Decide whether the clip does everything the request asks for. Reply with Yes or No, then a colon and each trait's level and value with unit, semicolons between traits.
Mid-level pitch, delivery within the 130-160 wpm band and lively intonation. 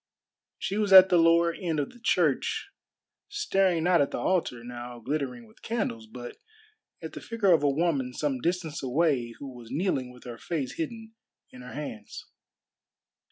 No: medium, 150 Hz; average, 170 wpm; wide, 6.5 semitones